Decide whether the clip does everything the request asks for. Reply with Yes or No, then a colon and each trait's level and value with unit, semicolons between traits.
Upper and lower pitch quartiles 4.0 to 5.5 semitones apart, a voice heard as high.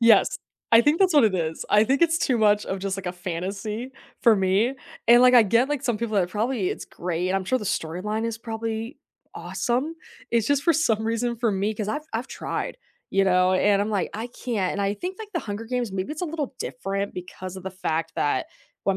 Yes: average, 4.3 semitones; high, 215 Hz